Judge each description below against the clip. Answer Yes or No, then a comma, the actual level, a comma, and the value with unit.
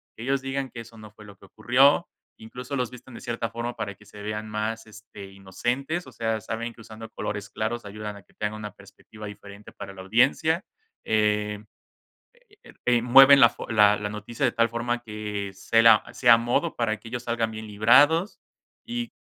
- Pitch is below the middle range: Yes, low, 110 Hz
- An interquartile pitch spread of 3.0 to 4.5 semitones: No, narrow, 2.5 semitones